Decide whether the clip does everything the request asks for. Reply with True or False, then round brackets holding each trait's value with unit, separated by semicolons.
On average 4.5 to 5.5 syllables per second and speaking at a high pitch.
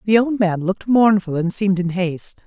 False (5.8 syllables/s; 195 Hz)